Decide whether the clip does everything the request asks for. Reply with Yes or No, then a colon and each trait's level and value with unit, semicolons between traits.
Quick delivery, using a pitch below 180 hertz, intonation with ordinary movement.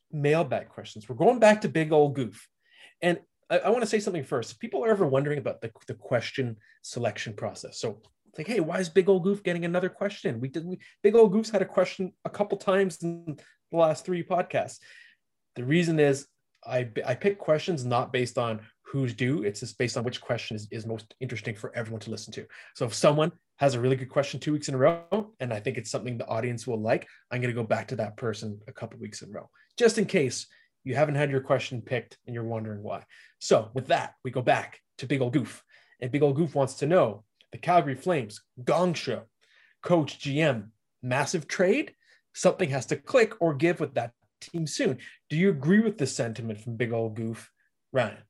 No: fast, 225 wpm; medium, 140 Hz; wide, 6.5 semitones